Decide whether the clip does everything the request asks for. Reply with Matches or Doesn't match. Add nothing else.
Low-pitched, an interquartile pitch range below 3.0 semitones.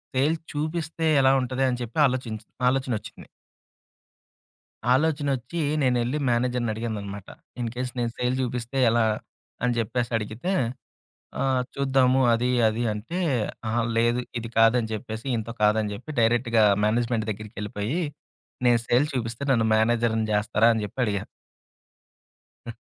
Matches